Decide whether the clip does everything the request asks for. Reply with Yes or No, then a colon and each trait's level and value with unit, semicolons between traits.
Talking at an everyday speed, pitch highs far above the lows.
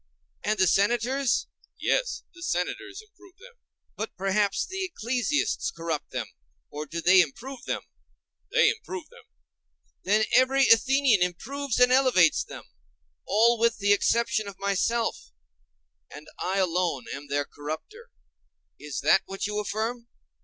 No: slow, 125 wpm; wide, 6.9 semitones